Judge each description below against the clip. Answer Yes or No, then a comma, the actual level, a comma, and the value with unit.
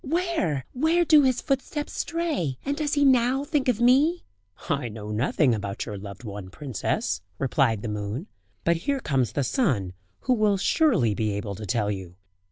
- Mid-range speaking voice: Yes, medium, 155 Hz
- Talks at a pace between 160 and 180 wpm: Yes, average, 175 wpm